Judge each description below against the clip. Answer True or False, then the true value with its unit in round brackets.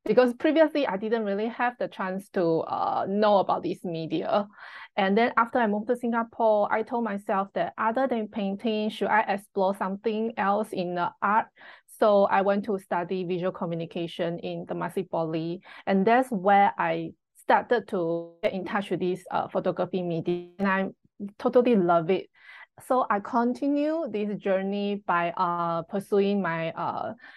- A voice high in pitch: True (200 Hz)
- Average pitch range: True (3.7 semitones)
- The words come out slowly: False (165 wpm)